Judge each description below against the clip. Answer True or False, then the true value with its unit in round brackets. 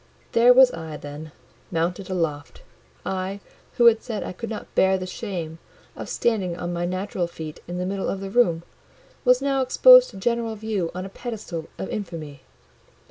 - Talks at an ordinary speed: True (180 wpm)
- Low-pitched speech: False (190 Hz)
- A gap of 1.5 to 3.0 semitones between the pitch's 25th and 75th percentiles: False (5.0 semitones)